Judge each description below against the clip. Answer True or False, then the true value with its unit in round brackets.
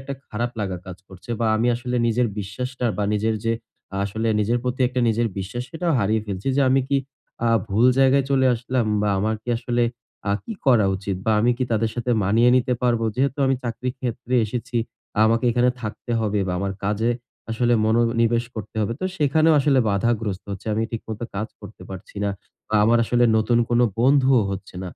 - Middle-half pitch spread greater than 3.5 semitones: False (2.9 semitones)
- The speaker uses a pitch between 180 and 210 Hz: False (115 Hz)